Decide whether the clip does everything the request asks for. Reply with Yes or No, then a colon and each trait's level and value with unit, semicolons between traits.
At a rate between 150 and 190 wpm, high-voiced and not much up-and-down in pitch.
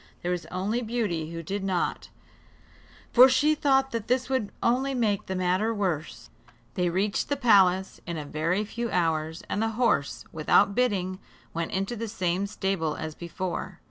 No: average, 170 wpm; high, 195 Hz; average, 5.1 semitones